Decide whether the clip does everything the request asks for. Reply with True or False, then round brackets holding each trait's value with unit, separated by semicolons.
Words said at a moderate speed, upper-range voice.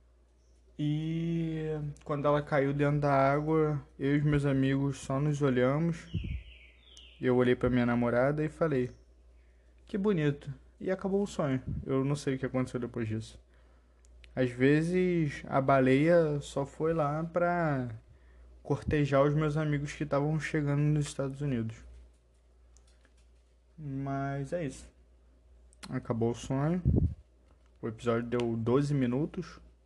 False (130 wpm; 135 Hz)